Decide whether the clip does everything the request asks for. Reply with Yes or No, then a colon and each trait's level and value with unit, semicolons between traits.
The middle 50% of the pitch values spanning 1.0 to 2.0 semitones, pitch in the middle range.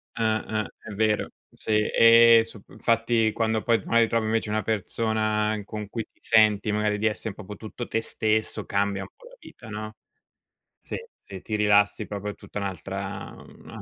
No: narrow, 1.4 semitones; low, 110 Hz